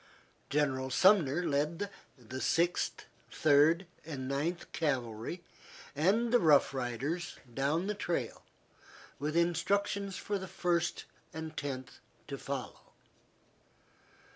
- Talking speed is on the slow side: Yes, slow, 105 wpm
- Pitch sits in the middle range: Yes, medium, 155 Hz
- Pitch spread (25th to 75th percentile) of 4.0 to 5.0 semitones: Yes, average, 4.5 semitones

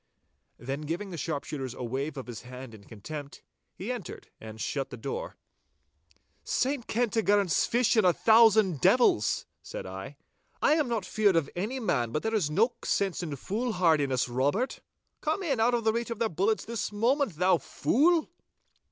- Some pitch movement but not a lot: No, wide, 8.7 semitones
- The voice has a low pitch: No, medium, 185 Hz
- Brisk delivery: No, average, 170 wpm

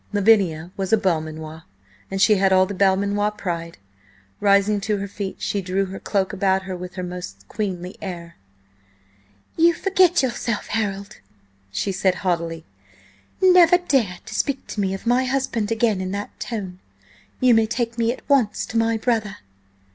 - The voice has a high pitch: Yes, high, 200 Hz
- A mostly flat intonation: No, average, 3.5 semitones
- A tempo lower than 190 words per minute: Yes, average, 165 wpm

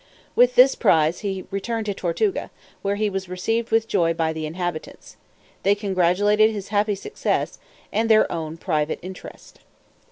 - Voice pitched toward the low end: No, high, 195 Hz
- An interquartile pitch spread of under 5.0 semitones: Yes, average, 4.0 semitones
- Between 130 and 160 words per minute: Yes, average, 155 wpm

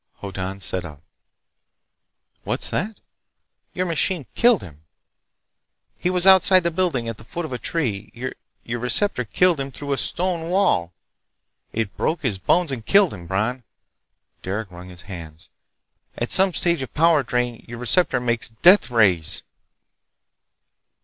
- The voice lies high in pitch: No, low, 125 Hz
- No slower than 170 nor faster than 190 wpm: No, average, 140 wpm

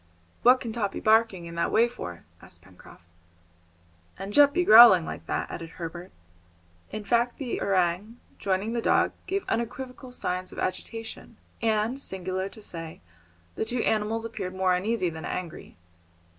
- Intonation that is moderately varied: Yes, average, 4.3 semitones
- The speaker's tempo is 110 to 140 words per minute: No, average, 155 wpm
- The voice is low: No, high, 210 Hz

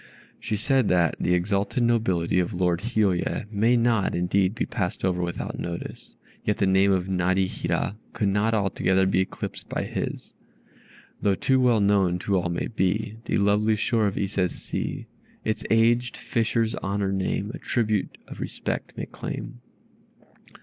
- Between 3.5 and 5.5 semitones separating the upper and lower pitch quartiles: No, average, 3.0 semitones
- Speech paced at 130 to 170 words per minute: Yes, average, 155 wpm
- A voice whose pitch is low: Yes, low, 100 Hz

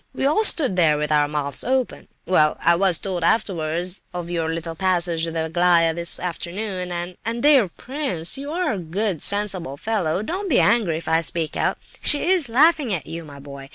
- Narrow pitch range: No, wide, 5.5 semitones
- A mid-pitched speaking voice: Yes, medium, 175 Hz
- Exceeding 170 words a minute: Yes, average, 180 wpm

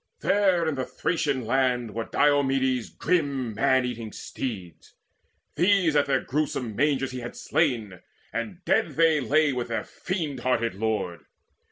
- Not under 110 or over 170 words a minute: Yes, average, 145 wpm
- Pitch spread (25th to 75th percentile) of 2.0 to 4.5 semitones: Yes, average, 4.2 semitones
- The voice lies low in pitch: Yes, low, 130 Hz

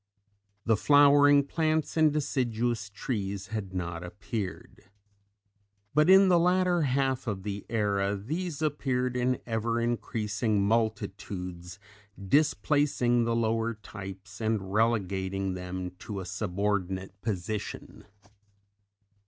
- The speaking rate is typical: No, slow, 105 wpm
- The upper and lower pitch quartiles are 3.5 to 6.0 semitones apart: Yes, average, 5.2 semitones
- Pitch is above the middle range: No, low, 110 Hz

